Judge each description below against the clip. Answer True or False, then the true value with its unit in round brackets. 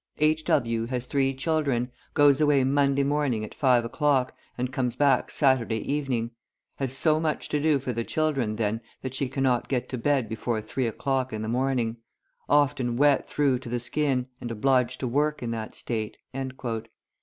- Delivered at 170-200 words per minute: True (180 wpm)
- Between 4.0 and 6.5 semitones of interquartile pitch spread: False (3.2 semitones)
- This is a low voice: True (130 Hz)